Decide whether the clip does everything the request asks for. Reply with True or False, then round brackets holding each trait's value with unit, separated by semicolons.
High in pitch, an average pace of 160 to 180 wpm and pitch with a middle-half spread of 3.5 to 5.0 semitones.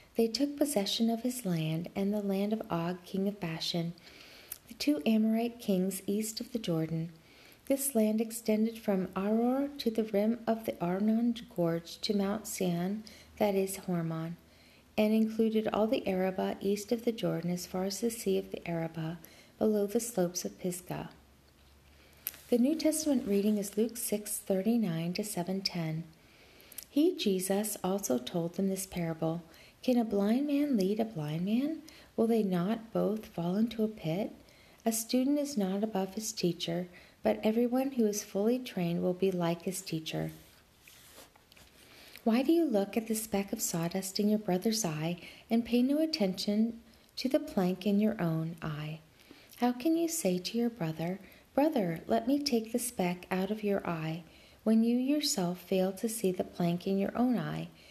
True (200 Hz; 175 wpm; 4.6 semitones)